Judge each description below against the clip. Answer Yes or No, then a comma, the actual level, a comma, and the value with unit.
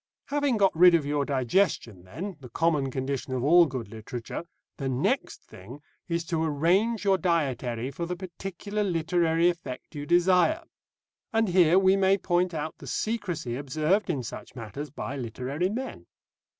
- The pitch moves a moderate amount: No, wide, 5.7 semitones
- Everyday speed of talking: Yes, average, 160 wpm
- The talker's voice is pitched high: No, medium, 165 Hz